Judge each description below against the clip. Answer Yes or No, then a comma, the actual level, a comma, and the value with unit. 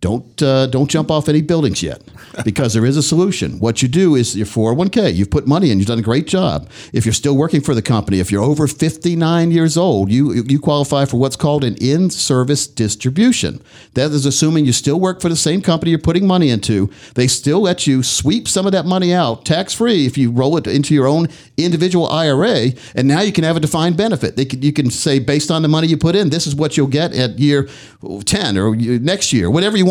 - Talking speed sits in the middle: No, fast, 240 wpm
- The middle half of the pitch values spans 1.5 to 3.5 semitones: No, average, 4.7 semitones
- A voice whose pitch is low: No, medium, 145 Hz